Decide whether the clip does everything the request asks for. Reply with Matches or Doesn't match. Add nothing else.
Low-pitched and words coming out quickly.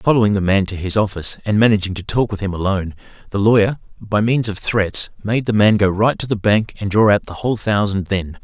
Matches